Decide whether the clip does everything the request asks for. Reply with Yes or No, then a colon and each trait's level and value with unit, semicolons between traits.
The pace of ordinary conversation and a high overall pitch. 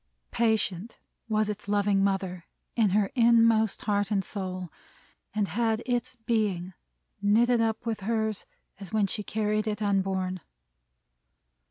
No: slow, 130 wpm; high, 210 Hz